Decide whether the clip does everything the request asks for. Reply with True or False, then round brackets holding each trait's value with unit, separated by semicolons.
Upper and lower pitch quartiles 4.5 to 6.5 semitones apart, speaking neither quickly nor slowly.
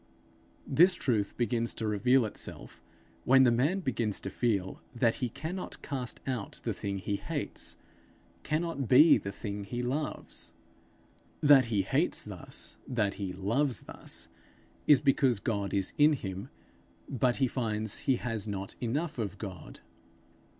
True (4.9 semitones; 145 wpm)